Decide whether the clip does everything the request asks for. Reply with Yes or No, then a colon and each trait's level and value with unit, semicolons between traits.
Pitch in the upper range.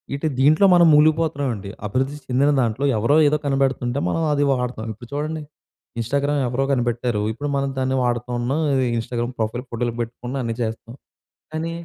No: low, 130 Hz